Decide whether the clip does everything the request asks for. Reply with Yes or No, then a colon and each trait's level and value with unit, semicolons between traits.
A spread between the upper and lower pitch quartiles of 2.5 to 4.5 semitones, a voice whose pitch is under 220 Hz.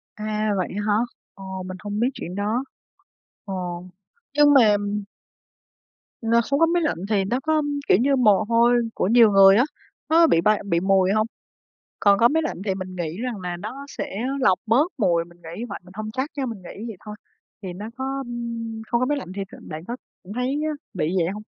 No: average, 5.0 semitones; high, 210 Hz